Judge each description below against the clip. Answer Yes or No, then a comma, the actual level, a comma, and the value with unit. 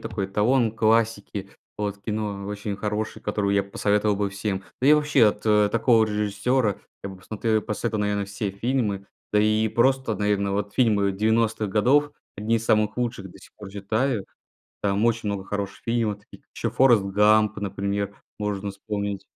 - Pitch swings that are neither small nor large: No, narrow, 1.9 semitones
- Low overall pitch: Yes, low, 105 Hz